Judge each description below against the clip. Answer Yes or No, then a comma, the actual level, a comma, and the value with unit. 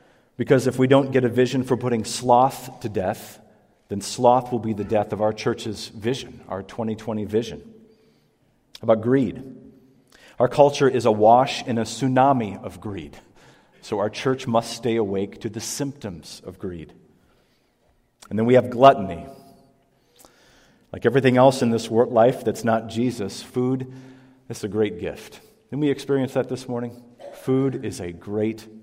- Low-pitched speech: Yes, low, 120 Hz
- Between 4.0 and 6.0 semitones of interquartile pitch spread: No, average, 3.2 semitones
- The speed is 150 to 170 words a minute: Yes, average, 160 wpm